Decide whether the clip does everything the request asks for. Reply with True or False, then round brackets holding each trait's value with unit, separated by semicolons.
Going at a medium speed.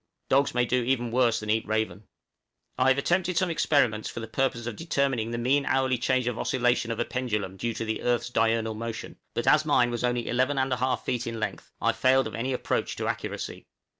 False (215 wpm)